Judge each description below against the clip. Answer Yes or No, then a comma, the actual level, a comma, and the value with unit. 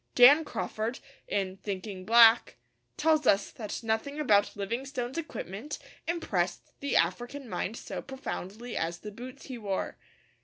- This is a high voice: Yes, high, 230 Hz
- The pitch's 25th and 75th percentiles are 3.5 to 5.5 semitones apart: Yes, average, 5.1 semitones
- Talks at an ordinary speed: No, slow, 130 wpm